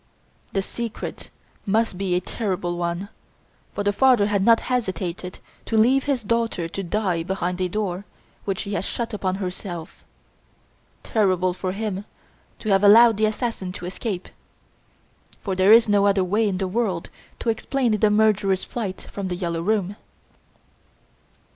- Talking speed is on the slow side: No, average, 155 wpm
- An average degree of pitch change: Yes, average, 3.0 semitones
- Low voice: No, high, 200 Hz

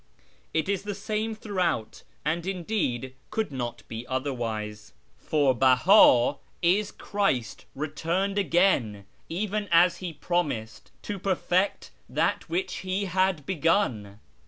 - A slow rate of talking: Yes, slow, 115 wpm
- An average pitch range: No, wide, 7.3 semitones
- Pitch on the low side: No, medium, 170 Hz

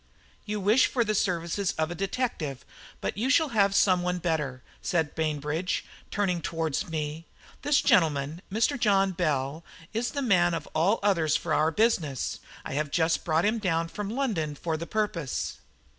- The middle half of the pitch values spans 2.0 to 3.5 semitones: No, average, 4.7 semitones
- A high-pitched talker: No, medium, 175 Hz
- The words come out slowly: No, average, 170 wpm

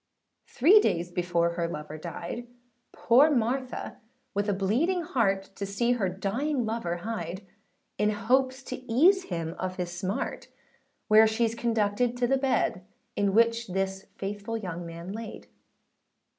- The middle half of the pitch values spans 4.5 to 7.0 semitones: Yes, average, 4.8 semitones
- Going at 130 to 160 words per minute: Yes, average, 145 wpm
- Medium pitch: No, high, 210 Hz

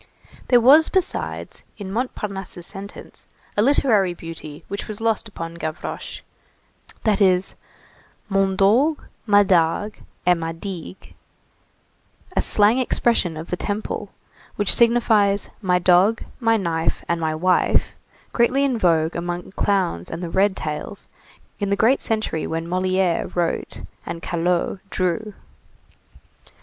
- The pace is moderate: No, slow, 130 wpm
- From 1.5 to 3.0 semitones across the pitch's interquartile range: No, average, 4.0 semitones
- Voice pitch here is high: Yes, high, 195 Hz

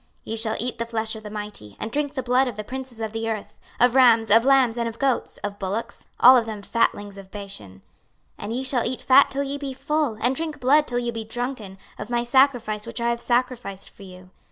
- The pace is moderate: No, fast, 250 wpm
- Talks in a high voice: Yes, high, 235 Hz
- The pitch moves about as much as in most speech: Yes, average, 3.4 semitones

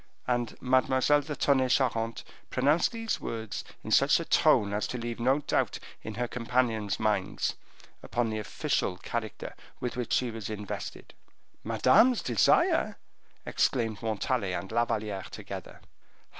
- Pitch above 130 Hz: No, low, 120 Hz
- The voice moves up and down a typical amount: Yes, average, 3.0 semitones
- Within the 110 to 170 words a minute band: Yes, average, 140 wpm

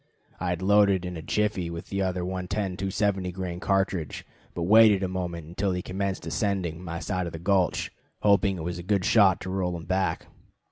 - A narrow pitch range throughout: Yes, narrow, 2.0 semitones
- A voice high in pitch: No, very low, 95 Hz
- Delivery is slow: No, average, 195 wpm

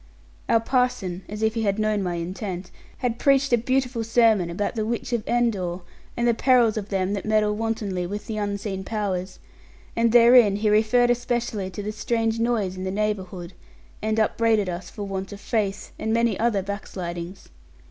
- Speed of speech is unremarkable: Yes, average, 180 wpm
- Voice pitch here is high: Yes, high, 215 Hz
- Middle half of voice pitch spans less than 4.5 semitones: Yes, average, 3.1 semitones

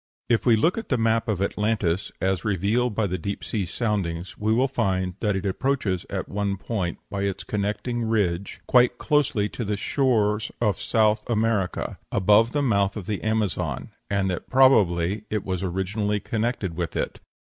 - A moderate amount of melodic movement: Yes, average, 3.0 semitones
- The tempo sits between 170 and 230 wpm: Yes, average, 175 wpm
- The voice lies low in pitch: Yes, low, 105 Hz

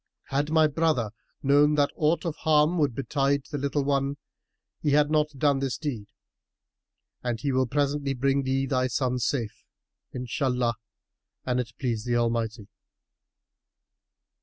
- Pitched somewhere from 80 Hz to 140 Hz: Yes, low, 135 Hz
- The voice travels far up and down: No, average, 2.9 semitones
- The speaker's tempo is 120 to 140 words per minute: Yes, slow, 135 wpm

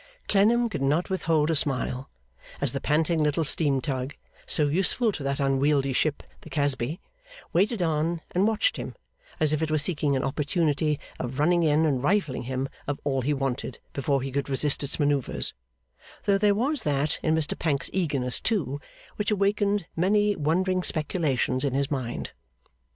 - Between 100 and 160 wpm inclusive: No, average, 170 wpm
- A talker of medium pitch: Yes, medium, 150 Hz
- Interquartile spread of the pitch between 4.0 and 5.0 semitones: Yes, average, 4.5 semitones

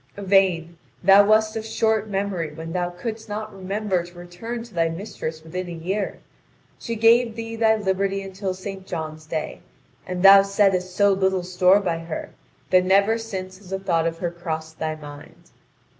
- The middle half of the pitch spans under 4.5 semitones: Yes, average, 3.0 semitones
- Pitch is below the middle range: No, high, 190 Hz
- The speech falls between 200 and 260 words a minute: No, average, 175 wpm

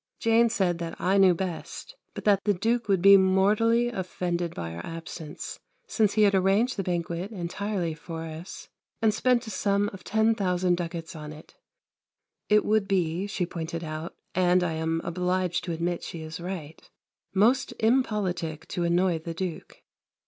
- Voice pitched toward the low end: No, medium, 180 Hz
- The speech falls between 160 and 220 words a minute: Yes, average, 165 wpm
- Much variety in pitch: No, average, 3.6 semitones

